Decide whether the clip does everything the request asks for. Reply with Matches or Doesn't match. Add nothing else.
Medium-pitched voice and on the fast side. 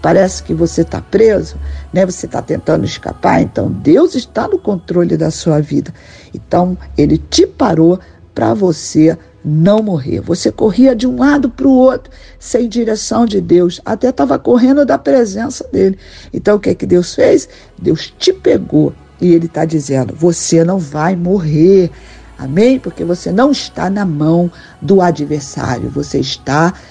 Doesn't match